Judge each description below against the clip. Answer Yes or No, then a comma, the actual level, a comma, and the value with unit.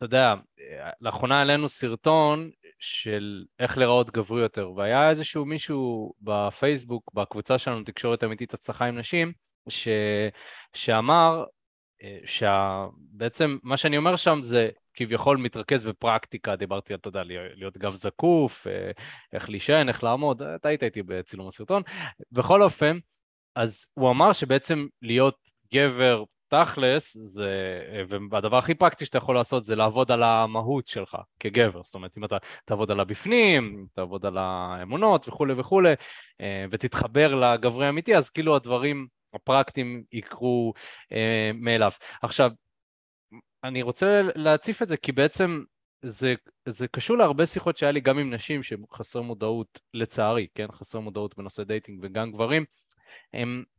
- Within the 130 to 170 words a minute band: Yes, average, 135 wpm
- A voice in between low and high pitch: No, low, 120 Hz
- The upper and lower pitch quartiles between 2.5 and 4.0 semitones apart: No, average, 5.3 semitones